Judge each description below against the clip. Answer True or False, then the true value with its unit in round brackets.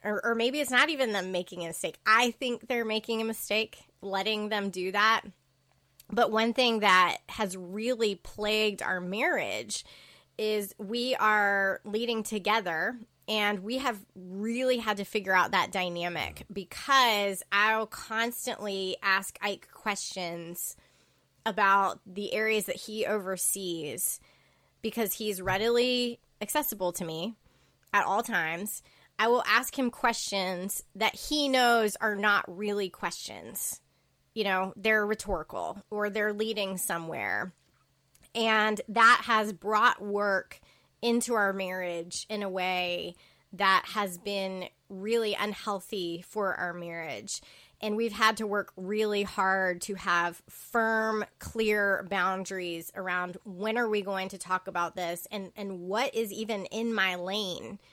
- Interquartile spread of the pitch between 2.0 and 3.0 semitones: True (2.7 semitones)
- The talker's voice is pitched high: True (205 Hz)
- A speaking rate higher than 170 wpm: False (140 wpm)